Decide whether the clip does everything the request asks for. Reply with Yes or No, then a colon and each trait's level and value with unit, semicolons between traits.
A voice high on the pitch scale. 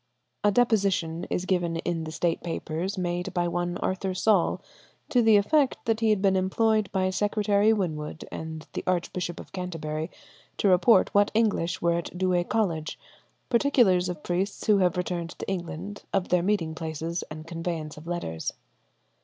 No: medium, 180 Hz